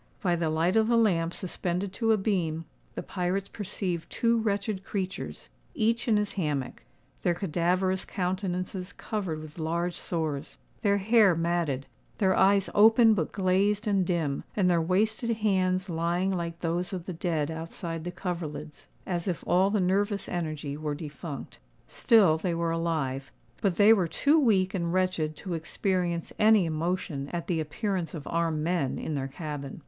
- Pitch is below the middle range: No, medium, 180 Hz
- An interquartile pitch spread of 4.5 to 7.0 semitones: No, average, 3.3 semitones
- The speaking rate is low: No, average, 165 wpm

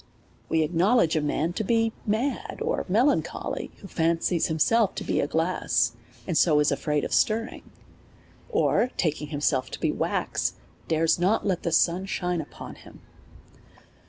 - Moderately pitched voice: Yes, medium, 175 Hz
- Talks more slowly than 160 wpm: Yes, average, 150 wpm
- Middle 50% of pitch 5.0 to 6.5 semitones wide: Yes, wide, 5.6 semitones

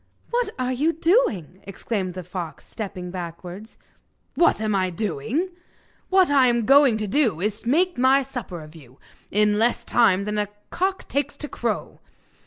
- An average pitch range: No, wide, 7.0 semitones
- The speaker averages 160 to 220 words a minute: Yes, average, 170 wpm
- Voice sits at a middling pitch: No, high, 220 Hz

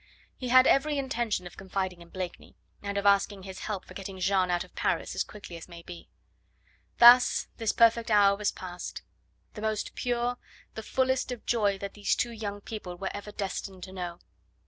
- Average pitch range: Yes, average, 3.7 semitones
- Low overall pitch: No, high, 200 Hz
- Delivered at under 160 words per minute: No, average, 190 wpm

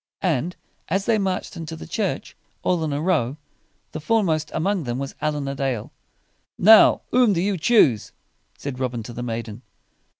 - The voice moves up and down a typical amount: No, wide, 6.6 semitones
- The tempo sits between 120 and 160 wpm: No, average, 175 wpm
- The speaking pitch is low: No, medium, 155 Hz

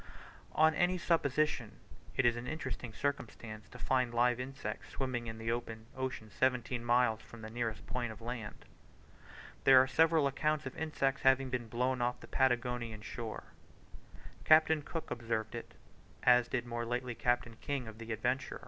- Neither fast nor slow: Yes, average, 165 wpm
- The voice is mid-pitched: No, low, 125 Hz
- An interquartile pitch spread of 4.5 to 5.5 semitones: No, narrow, 2.5 semitones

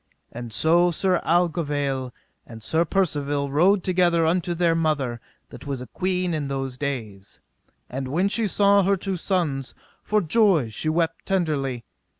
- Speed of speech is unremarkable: Yes, average, 155 wpm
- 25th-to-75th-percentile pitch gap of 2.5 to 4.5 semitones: No, average, 4.9 semitones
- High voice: No, medium, 160 Hz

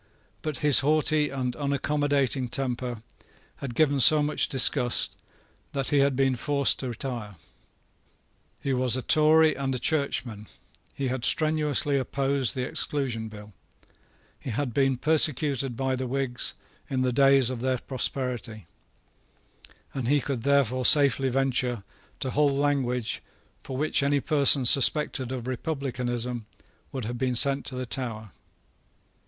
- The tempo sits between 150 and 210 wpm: No, average, 140 wpm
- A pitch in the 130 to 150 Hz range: Yes, low, 135 Hz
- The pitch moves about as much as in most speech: No, narrow, 2.3 semitones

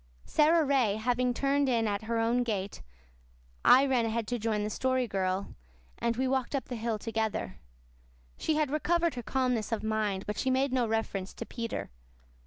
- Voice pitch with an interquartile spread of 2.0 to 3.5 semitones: Yes, average, 3.2 semitones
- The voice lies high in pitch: Yes, high, 235 Hz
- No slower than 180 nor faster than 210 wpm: Yes, average, 185 wpm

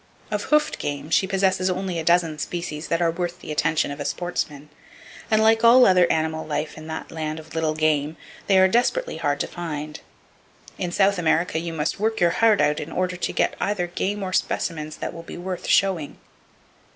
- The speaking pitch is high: No, medium, 170 Hz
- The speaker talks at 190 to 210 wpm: Yes, average, 200 wpm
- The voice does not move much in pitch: No, average, 3.3 semitones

